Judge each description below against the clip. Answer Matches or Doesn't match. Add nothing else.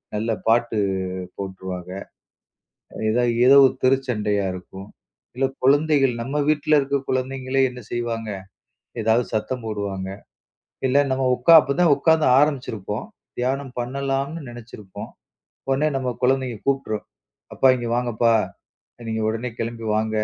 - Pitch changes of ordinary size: Matches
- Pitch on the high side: Doesn't match